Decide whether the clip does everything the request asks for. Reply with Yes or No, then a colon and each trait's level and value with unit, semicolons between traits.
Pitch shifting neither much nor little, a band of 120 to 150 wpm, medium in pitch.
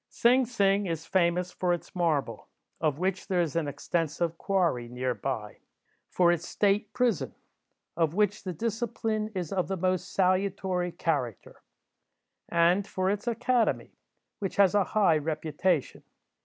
Yes: average, 3.4 semitones; average, 140 wpm; medium, 180 Hz